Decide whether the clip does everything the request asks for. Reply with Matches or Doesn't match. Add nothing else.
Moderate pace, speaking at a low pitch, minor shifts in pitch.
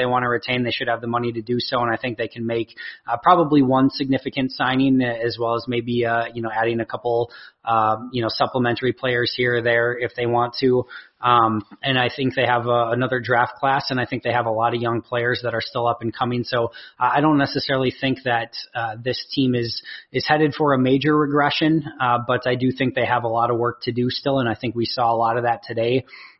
Doesn't match